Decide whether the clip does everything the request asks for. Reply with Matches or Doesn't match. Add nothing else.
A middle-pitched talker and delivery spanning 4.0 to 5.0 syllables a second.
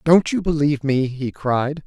Matches